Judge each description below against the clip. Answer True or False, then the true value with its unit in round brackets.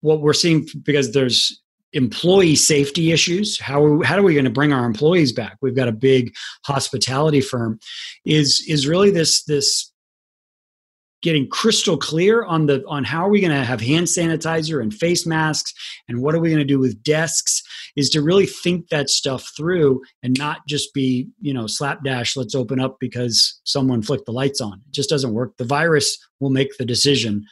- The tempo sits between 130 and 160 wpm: False (190 wpm)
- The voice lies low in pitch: False (145 Hz)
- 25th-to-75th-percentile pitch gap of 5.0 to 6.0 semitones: False (3.7 semitones)